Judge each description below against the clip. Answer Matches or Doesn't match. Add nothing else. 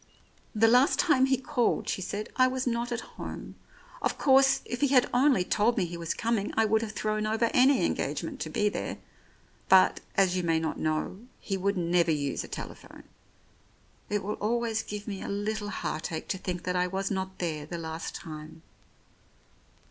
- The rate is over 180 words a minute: Matches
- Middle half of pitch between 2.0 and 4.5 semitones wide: Doesn't match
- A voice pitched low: Doesn't match